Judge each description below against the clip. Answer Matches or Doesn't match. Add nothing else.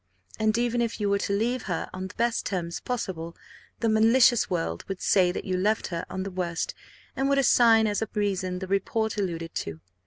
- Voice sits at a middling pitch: Doesn't match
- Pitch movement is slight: Doesn't match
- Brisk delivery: Matches